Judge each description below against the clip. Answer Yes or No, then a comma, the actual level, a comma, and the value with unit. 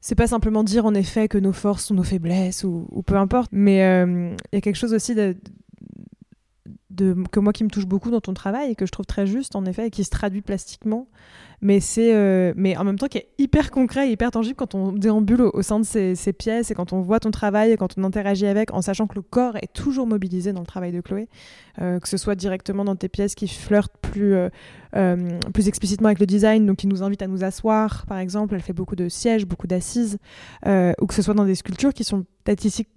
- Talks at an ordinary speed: No, fast, 255 wpm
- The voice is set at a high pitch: Yes, high, 200 Hz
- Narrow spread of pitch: Yes, narrow, 2.2 semitones